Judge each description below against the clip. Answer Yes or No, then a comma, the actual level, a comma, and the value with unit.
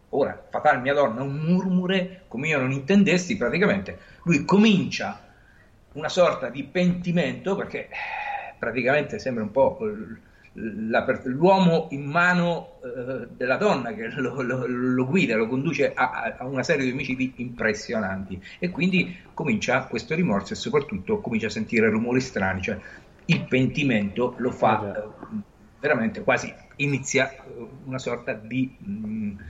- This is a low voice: No, medium, 150 Hz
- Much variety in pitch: Yes, wide, 6.9 semitones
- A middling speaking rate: Yes, average, 130 wpm